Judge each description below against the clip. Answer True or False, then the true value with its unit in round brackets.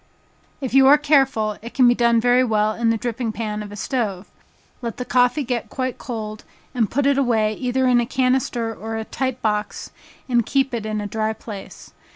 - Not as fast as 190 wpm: False (200 wpm)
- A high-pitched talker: True (235 Hz)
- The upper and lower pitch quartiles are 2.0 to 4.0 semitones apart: True (3.0 semitones)